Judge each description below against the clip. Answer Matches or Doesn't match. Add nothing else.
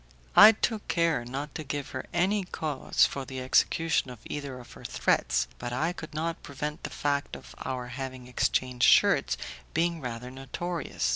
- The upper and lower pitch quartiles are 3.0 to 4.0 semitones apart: Doesn't match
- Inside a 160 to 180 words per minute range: Matches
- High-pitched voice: Doesn't match